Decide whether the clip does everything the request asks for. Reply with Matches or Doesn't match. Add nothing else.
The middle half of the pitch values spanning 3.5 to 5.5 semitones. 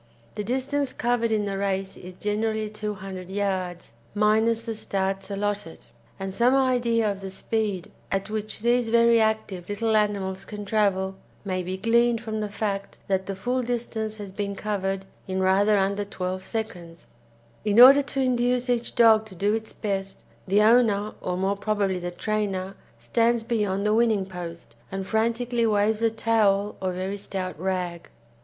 Doesn't match